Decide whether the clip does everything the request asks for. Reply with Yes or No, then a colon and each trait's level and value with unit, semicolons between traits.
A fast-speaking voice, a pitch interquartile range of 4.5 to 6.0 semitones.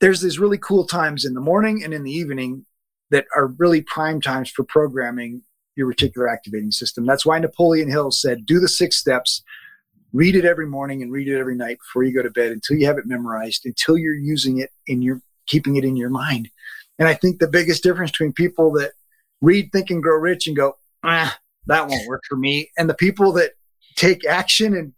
Yes: fast, 220 wpm; average, 4.8 semitones